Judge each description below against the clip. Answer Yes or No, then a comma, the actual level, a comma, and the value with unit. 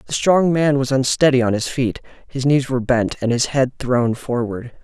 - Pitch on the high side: No, low, 130 Hz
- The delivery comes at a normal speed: No, fast, 210 wpm